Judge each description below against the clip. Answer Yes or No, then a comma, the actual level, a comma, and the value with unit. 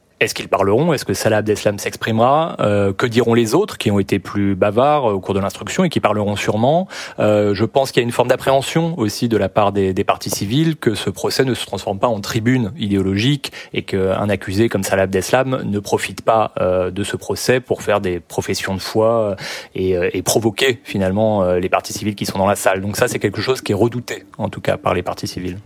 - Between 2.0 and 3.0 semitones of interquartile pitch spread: No, average, 3.6 semitones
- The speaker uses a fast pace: Yes, fast, 230 wpm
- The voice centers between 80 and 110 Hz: Yes, low, 105 Hz